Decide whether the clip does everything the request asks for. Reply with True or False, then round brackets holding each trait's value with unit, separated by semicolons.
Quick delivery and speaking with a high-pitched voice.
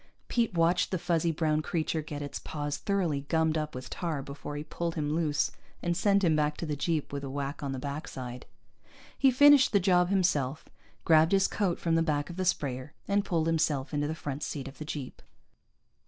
False (210 wpm; 155 Hz)